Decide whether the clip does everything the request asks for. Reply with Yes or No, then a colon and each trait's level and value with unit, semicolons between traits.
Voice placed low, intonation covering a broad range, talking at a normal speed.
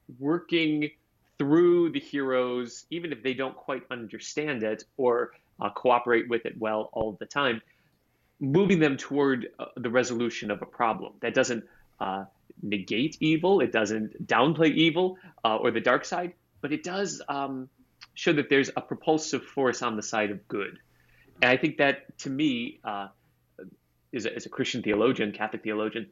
Yes: low, 130 Hz; wide, 5.9 semitones; average, 170 wpm